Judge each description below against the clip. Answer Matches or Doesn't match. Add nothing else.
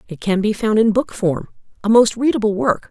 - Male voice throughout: Doesn't match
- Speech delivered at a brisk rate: Matches